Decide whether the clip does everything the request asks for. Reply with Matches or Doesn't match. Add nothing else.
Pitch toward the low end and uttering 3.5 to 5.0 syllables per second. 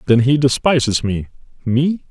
Matches